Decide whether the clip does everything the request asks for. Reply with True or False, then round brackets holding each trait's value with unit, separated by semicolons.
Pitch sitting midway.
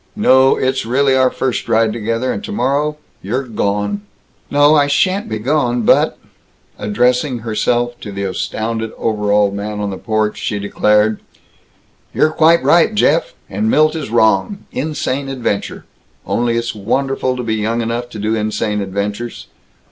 False (115 Hz)